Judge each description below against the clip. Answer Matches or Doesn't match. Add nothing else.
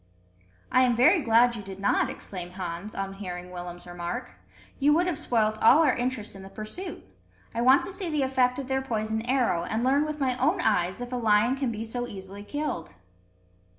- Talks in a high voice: Matches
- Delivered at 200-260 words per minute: Matches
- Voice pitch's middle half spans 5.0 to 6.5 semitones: Matches